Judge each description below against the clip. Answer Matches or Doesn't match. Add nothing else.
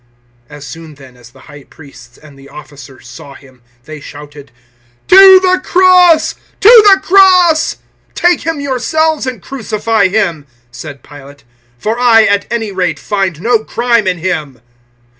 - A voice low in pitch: Doesn't match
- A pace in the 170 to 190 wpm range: Doesn't match